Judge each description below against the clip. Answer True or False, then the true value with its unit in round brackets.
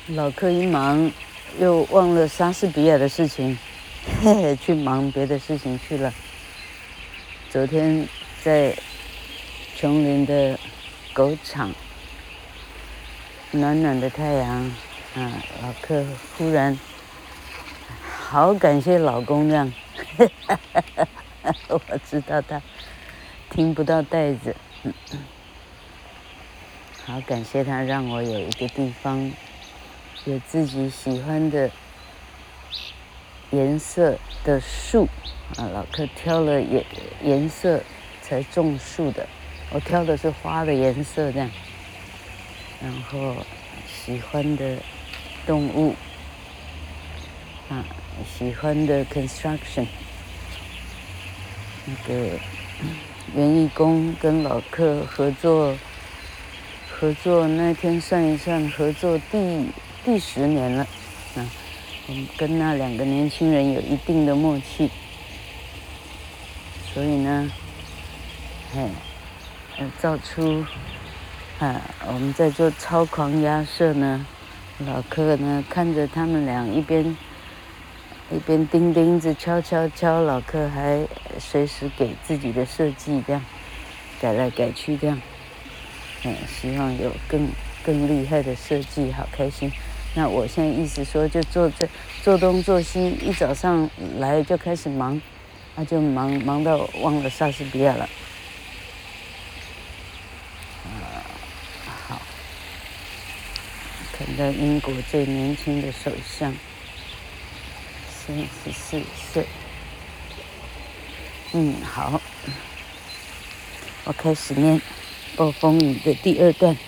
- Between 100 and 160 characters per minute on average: True (155 characters per minute)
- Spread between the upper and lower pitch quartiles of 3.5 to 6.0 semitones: False (9.0 semitones)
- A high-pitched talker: False (135 Hz)